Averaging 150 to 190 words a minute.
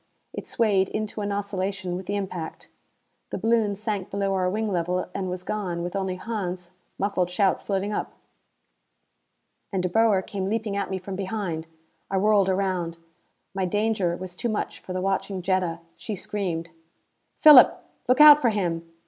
Yes: average, 165 wpm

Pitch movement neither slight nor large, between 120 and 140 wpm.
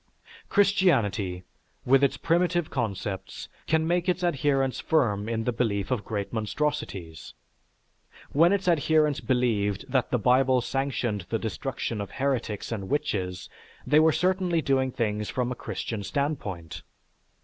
No: wide, 6.5 semitones; slow, 135 wpm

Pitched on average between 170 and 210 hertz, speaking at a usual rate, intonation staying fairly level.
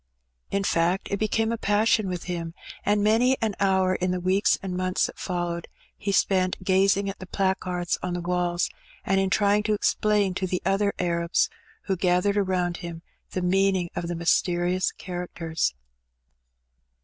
Yes: medium, 185 Hz; average, 165 wpm; narrow, 2.0 semitones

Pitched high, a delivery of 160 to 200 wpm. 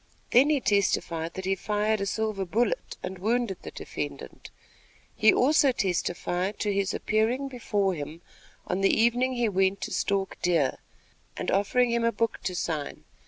Yes: high, 205 Hz; average, 165 wpm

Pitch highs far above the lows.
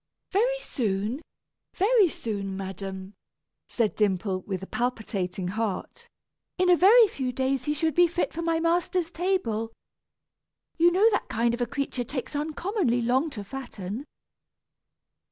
Yes: wide, 8.4 semitones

